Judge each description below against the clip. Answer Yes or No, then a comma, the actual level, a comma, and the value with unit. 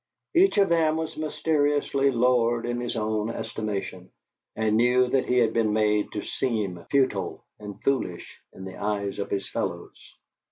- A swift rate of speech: No, average, 160 wpm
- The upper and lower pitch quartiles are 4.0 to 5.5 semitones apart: Yes, average, 4.6 semitones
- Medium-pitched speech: No, low, 115 Hz